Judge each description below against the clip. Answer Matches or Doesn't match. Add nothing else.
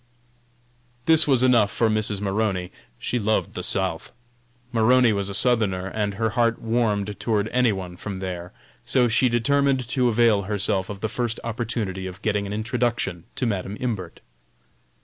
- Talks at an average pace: Matches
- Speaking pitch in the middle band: Doesn't match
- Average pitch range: Matches